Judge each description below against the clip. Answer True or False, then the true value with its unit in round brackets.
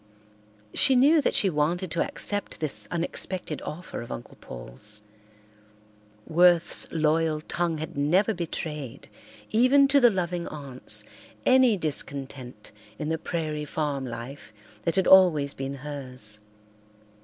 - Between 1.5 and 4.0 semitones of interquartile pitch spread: False (4.5 semitones)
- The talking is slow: True (125 wpm)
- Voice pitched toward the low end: False (155 Hz)